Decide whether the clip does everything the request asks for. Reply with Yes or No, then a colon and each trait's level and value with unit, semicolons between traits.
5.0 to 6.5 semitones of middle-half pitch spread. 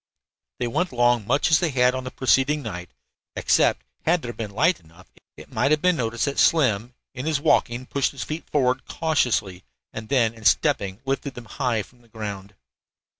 No: average, 4.3 semitones